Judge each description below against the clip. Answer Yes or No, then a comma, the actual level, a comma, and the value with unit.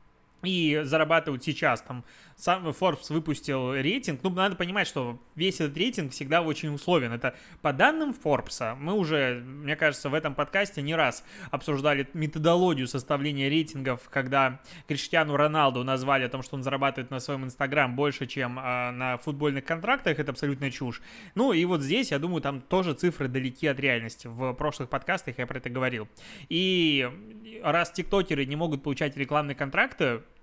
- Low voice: No, medium, 145 Hz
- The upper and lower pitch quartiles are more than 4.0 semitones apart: No, average, 3.7 semitones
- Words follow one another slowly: No, fast, 160 wpm